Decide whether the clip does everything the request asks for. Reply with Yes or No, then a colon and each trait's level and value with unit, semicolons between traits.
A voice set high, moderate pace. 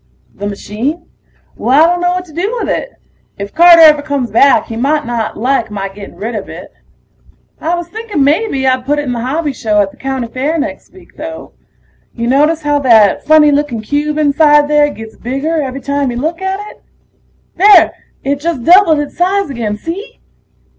Yes: very high, 290 Hz; average, 195 wpm